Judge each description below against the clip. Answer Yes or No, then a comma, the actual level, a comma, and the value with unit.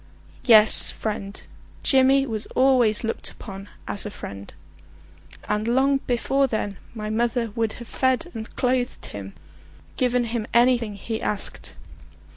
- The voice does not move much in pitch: No, average, 3.1 semitones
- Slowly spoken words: Yes, slow, 130 wpm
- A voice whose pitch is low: No, high, 230 Hz